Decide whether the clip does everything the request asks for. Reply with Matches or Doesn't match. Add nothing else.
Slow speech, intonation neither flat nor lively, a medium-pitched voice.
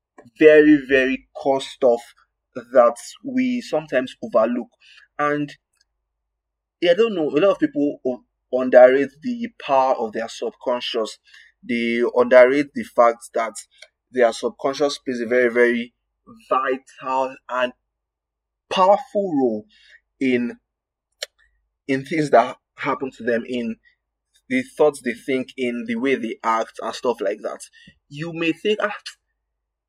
Doesn't match